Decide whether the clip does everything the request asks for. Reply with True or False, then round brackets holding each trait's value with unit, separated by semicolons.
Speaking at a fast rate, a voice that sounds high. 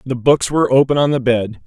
False (255 wpm; 125 Hz)